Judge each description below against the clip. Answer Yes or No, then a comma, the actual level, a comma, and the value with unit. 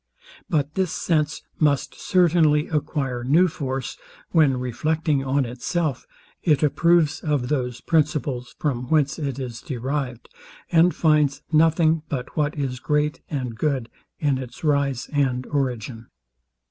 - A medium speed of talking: No, slow, 130 wpm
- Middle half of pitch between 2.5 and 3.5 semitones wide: Yes, average, 3.2 semitones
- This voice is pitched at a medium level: Yes, medium, 145 Hz